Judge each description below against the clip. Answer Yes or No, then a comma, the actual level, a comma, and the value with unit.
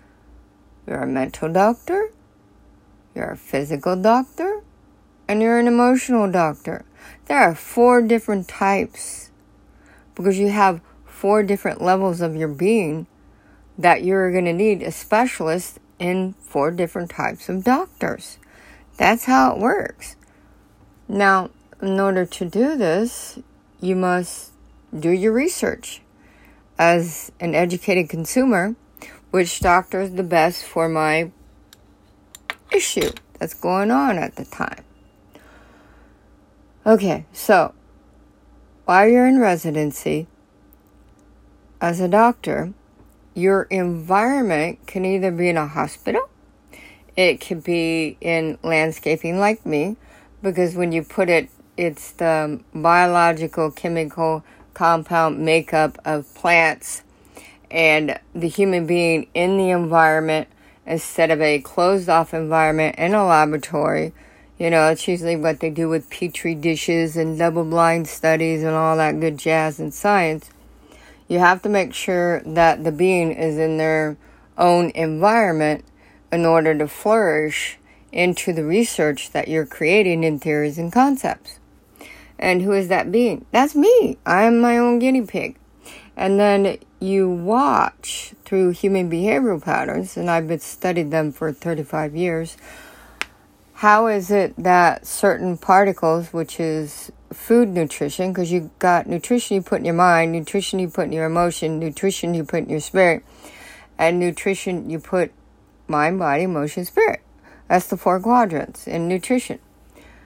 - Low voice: No, medium, 170 Hz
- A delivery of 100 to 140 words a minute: Yes, slow, 135 wpm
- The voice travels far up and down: No, average, 3.6 semitones